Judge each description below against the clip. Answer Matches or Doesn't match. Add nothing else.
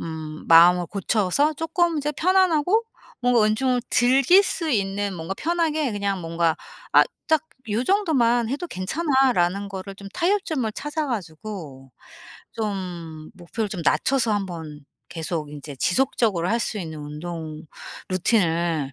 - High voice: Matches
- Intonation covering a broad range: Matches